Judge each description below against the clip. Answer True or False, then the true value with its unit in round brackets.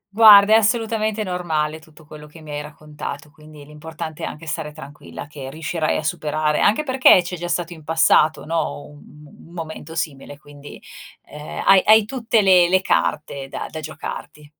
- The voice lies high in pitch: False (155 Hz)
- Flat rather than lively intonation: False (3.4 semitones)